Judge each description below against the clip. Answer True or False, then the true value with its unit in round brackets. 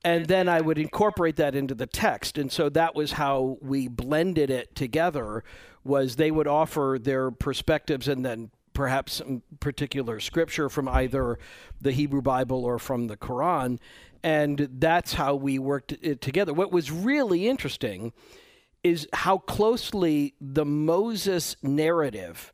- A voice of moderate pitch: True (145 Hz)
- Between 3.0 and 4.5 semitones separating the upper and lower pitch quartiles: True (3.6 semitones)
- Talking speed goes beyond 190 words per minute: False (150 wpm)